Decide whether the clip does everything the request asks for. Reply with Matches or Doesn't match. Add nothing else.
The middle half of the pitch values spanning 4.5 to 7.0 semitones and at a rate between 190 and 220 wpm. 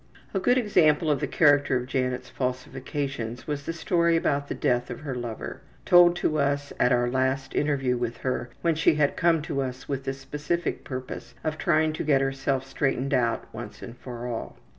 Doesn't match